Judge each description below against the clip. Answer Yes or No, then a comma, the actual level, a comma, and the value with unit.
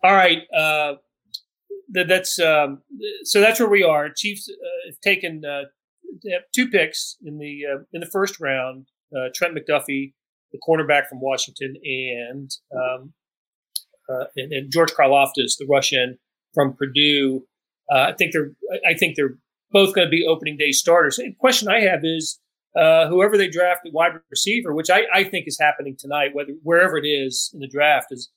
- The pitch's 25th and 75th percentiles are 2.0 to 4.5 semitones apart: No, average, 5.2 semitones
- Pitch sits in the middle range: Yes, medium, 155 Hz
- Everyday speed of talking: Yes, average, 180 wpm